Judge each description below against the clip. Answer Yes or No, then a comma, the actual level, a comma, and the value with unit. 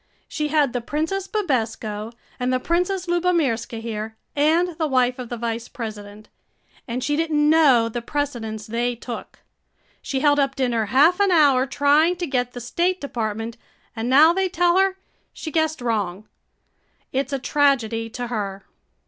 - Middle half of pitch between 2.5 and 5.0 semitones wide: No, wide, 5.5 semitones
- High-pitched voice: Yes, very high, 260 Hz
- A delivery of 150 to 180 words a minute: Yes, average, 165 wpm